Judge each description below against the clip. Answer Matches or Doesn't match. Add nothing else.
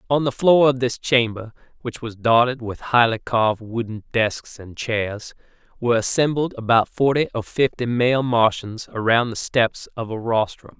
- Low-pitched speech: Matches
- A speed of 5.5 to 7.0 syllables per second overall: Doesn't match